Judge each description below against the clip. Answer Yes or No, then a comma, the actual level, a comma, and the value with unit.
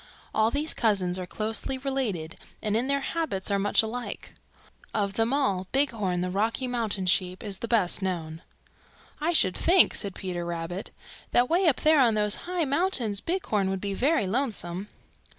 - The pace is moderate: Yes, average, 170 wpm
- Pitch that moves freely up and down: Yes, wide, 6.1 semitones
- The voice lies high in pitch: Yes, high, 215 Hz